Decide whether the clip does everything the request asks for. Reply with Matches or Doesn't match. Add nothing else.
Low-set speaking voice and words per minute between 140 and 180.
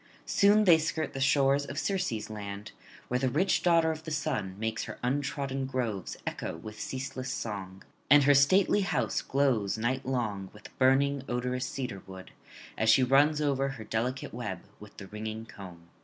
Matches